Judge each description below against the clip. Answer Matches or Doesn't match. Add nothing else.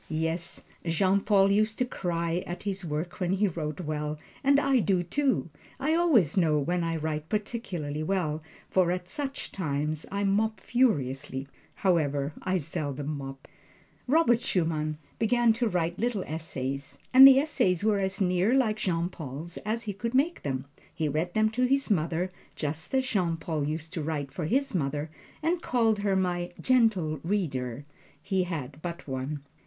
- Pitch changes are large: Matches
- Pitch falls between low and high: Matches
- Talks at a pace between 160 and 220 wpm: Matches